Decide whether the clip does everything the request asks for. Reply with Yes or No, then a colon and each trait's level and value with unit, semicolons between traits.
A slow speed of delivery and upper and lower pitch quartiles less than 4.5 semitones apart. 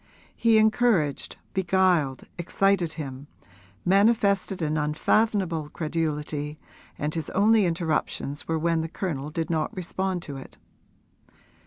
Yes: slow, 115 wpm; average, 4.1 semitones